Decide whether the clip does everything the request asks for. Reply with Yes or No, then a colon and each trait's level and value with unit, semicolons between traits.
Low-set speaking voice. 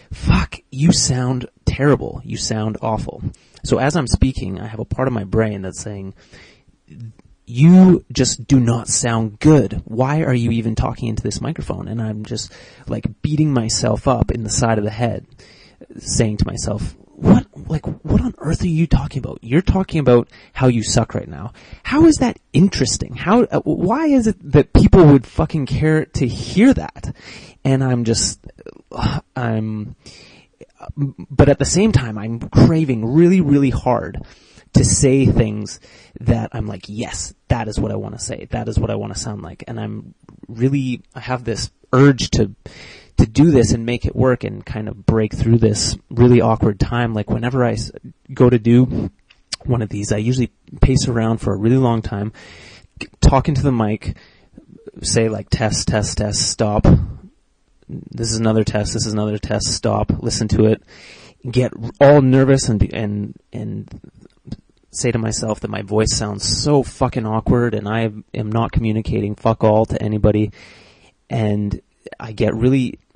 Yes: low, 115 Hz